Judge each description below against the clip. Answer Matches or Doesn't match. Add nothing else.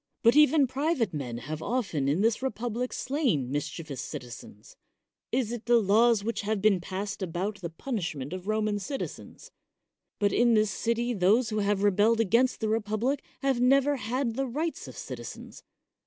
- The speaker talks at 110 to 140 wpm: Doesn't match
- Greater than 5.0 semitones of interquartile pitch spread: Doesn't match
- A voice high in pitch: Matches